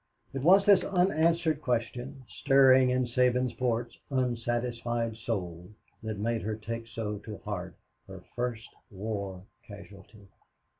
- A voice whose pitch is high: No, low, 120 Hz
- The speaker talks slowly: Yes, slow, 115 wpm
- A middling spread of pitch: Yes, average, 3.1 semitones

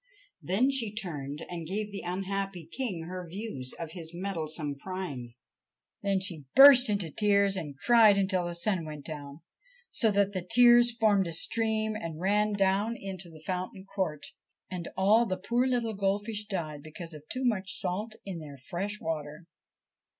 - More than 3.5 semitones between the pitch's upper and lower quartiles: Yes, average, 4.3 semitones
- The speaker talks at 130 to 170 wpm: Yes, average, 165 wpm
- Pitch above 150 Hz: Yes, high, 190 Hz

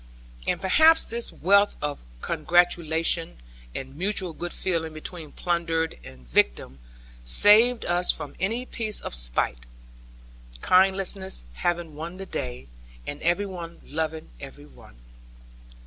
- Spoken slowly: Yes, slow, 120 wpm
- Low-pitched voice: No, medium, 170 Hz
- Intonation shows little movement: No, average, 4.3 semitones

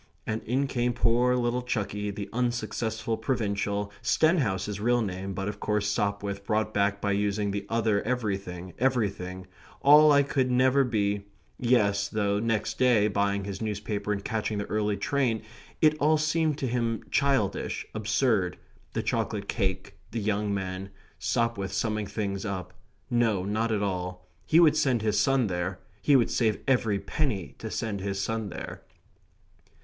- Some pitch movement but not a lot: Yes, average, 3.4 semitones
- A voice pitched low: Yes, low, 105 Hz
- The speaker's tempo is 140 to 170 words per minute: Yes, average, 155 wpm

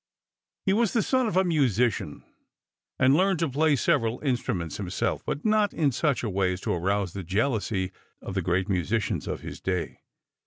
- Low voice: Yes, low, 120 Hz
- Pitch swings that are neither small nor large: No, wide, 8.9 semitones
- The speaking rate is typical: Yes, average, 185 wpm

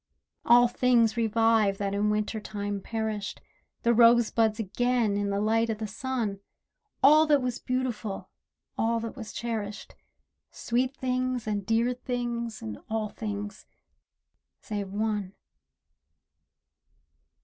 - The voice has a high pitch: Yes, high, 225 Hz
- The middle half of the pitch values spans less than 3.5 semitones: Yes, narrow, 2.6 semitones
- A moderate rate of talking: No, slow, 120 wpm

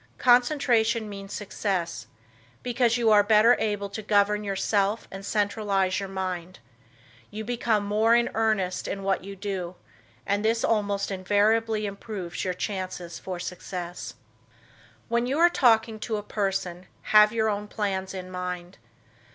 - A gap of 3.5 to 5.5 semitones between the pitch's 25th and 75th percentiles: No, average, 2.7 semitones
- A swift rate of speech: No, average, 145 wpm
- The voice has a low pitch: No, high, 205 Hz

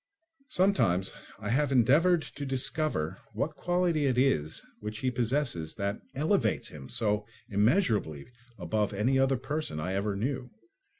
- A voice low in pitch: Yes, low, 125 Hz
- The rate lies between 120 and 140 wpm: Yes, slow, 135 wpm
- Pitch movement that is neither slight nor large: No, wide, 6.2 semitones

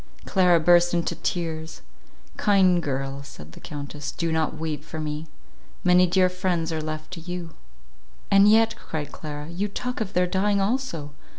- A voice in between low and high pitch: Yes, medium, 170 Hz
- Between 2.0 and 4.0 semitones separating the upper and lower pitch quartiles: Yes, average, 3.2 semitones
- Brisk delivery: No, average, 165 wpm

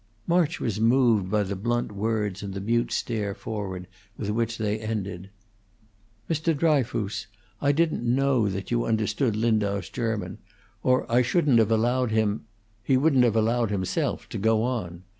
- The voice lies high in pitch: No, low, 110 Hz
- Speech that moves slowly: No, average, 160 wpm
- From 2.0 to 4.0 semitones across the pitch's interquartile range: Yes, average, 3.1 semitones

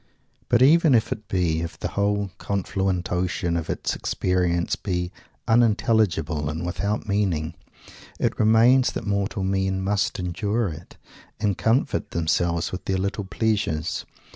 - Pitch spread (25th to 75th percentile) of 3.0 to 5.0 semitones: Yes, average, 3.5 semitones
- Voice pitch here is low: Yes, very low, 95 Hz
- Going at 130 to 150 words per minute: Yes, average, 140 wpm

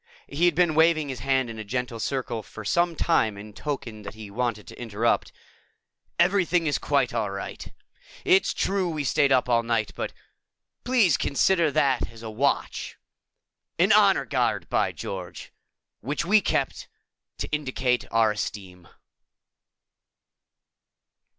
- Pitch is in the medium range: No, low, 130 Hz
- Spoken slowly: No, average, 145 wpm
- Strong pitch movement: Yes, wide, 6.6 semitones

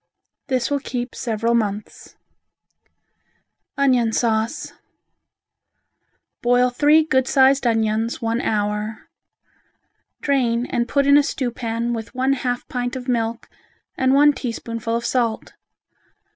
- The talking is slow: Yes, slow, 115 wpm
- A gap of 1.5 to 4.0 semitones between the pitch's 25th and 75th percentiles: Yes, narrow, 2.5 semitones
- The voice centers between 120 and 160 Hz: No, high, 245 Hz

